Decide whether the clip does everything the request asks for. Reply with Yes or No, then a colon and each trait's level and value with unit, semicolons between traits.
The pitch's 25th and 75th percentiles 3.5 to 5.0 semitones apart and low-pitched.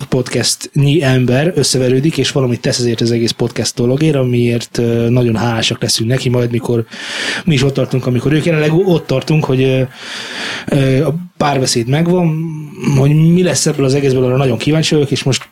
Yes: average, 3.9 semitones; low, 130 Hz